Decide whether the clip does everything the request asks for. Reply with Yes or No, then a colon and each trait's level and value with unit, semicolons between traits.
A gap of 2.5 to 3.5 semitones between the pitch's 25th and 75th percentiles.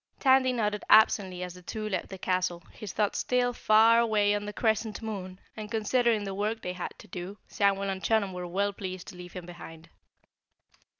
Yes: average, 3.1 semitones